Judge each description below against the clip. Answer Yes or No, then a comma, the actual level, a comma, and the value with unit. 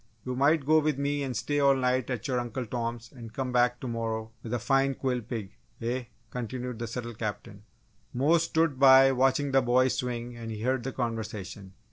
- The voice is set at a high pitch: No, low, 125 Hz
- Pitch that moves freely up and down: No, narrow, 2.4 semitones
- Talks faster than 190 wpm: Yes, average, 200 wpm